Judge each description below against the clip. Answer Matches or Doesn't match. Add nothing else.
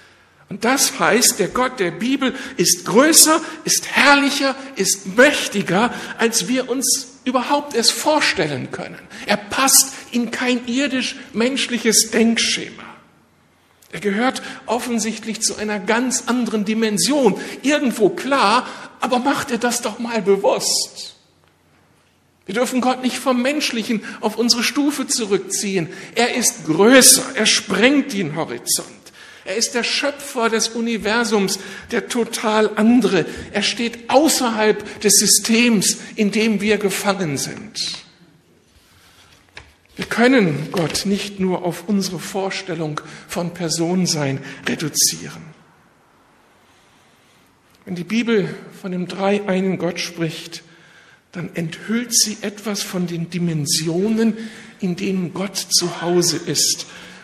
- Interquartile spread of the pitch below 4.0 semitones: Doesn't match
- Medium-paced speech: Doesn't match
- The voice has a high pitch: Matches